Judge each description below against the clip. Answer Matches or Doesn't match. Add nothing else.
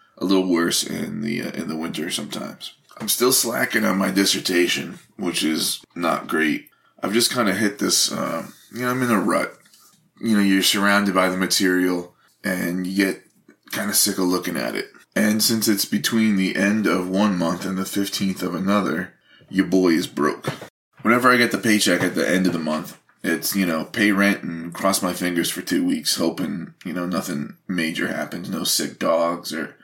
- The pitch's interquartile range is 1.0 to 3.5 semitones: Matches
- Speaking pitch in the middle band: Doesn't match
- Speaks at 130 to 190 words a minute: Doesn't match